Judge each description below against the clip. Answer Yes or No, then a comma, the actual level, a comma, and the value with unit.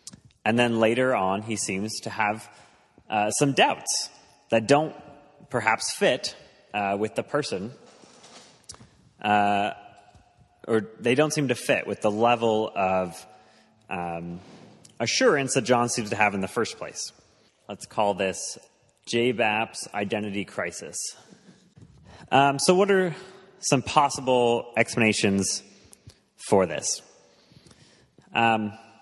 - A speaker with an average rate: No, slow, 120 wpm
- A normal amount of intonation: Yes, average, 3.6 semitones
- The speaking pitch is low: Yes, low, 110 Hz